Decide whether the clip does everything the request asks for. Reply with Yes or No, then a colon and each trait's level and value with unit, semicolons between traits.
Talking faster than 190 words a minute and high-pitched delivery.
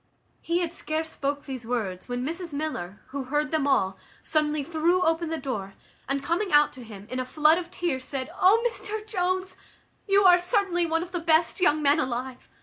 Yes: average, 200 wpm; very high, 310 Hz